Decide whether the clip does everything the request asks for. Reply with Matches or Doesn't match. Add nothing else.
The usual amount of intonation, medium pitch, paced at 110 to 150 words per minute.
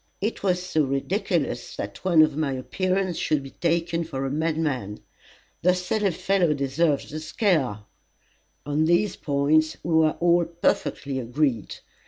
Matches